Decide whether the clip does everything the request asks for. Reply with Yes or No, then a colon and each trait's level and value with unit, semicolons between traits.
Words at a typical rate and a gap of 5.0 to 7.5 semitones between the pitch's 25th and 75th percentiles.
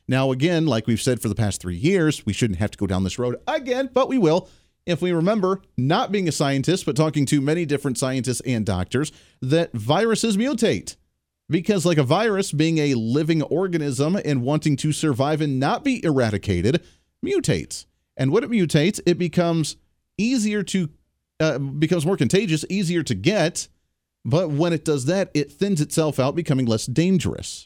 Yes: average, 180 wpm; wide, 5.5 semitones